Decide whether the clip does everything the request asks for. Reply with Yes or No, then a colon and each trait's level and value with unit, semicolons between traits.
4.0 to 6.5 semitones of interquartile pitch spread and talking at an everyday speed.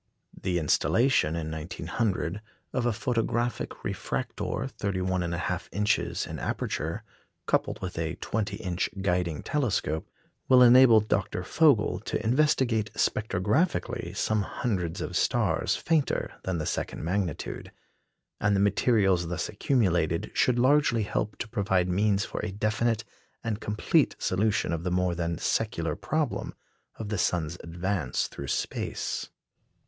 No: average, 4.4 semitones; slow, 130 wpm